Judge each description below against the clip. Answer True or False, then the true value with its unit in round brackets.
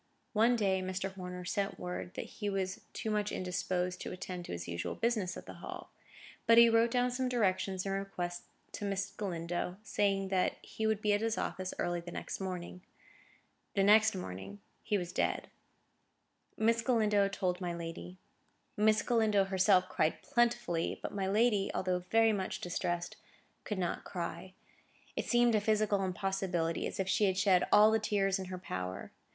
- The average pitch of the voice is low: False (195 Hz)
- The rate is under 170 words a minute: False (175 wpm)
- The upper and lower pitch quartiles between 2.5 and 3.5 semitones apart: True (2.9 semitones)